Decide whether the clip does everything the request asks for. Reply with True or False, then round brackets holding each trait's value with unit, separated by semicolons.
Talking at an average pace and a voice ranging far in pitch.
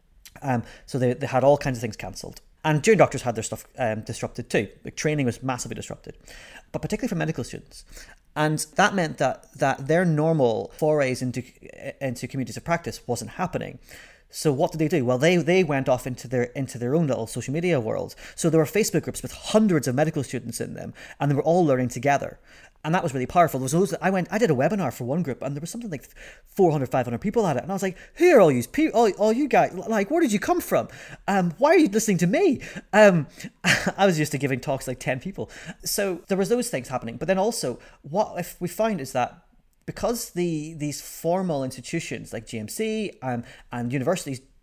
False (230 wpm; 6.4 semitones)